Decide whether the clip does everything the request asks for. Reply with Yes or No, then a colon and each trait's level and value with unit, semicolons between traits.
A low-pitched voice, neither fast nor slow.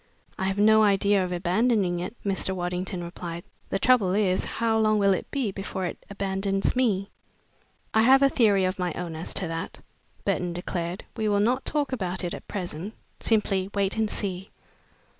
No: high, 195 Hz; average, 180 wpm